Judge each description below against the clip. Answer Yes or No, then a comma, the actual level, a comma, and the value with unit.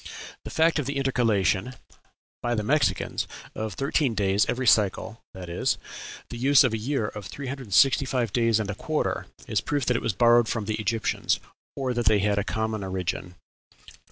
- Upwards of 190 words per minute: Yes, average, 200 wpm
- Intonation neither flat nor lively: Yes, average, 4.1 semitones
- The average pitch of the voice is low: Yes, low, 115 Hz